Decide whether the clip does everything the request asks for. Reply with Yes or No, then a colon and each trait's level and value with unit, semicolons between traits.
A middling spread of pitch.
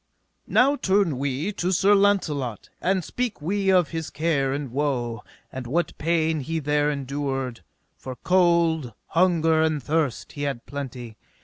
Yes: average, 4.4 semitones